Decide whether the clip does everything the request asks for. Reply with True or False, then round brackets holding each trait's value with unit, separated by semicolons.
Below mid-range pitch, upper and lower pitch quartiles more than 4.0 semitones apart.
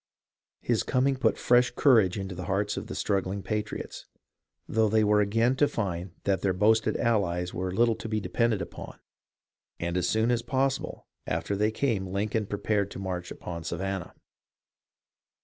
False (105 Hz; 3.4 semitones)